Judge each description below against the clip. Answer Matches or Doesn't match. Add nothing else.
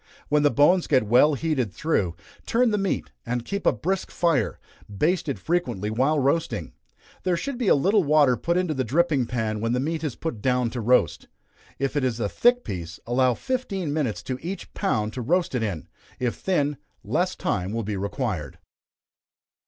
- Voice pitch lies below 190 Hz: Matches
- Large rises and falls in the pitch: Matches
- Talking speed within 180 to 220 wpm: Matches